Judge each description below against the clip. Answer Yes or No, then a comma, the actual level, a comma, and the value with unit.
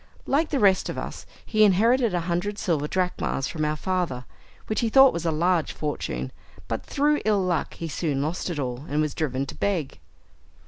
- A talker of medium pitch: Yes, medium, 175 Hz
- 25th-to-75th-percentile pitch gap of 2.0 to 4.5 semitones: No, wide, 5.4 semitones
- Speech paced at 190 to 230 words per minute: Yes, average, 195 wpm